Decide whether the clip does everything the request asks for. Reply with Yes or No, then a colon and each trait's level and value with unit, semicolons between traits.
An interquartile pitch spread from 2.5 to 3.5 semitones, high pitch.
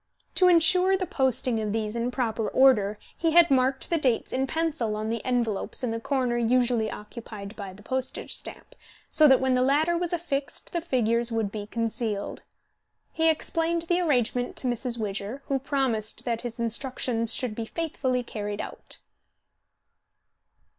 No: average, 4.0 semitones; very high, 250 Hz